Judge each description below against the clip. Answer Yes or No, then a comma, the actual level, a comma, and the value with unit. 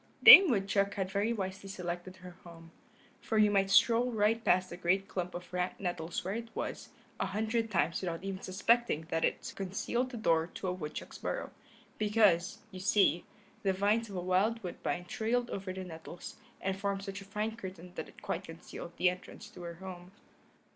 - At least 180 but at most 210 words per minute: Yes, average, 190 wpm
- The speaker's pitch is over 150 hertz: Yes, high, 190 Hz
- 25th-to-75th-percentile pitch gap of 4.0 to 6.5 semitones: No, average, 2.9 semitones